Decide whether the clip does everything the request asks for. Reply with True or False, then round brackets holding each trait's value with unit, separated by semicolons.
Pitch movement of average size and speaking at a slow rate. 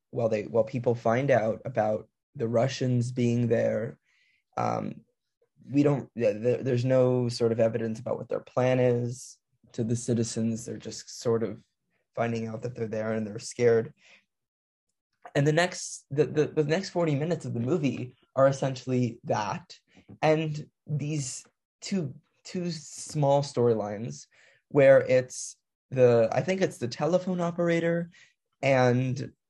False (4.0 semitones; 145 wpm)